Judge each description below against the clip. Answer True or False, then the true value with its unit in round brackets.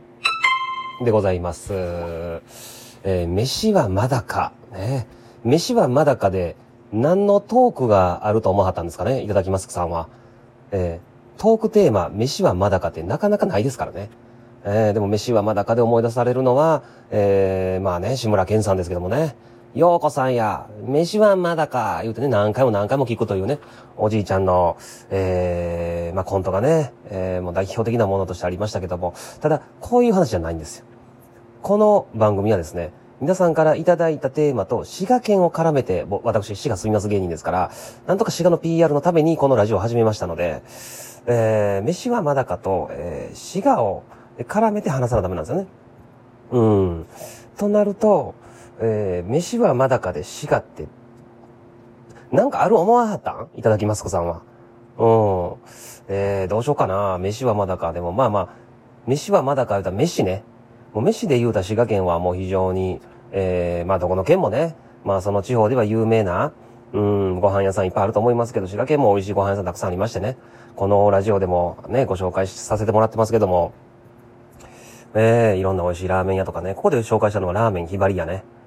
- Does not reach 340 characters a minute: False (370 characters per minute)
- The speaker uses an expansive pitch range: False (5.0 semitones)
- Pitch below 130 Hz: True (115 Hz)